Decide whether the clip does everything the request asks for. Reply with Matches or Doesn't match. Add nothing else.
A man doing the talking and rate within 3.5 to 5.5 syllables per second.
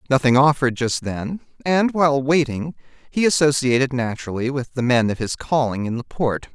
Matches